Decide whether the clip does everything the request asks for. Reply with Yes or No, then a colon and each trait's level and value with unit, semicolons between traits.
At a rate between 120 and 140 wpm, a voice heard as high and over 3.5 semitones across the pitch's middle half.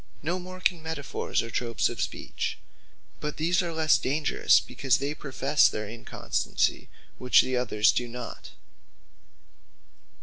No: slow, 135 wpm; medium, 140 Hz; average, 4.9 semitones